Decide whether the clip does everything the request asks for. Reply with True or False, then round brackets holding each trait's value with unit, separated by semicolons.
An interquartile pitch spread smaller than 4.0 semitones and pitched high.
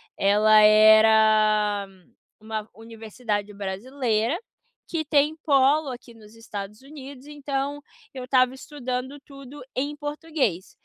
False (4.7 semitones; 245 Hz)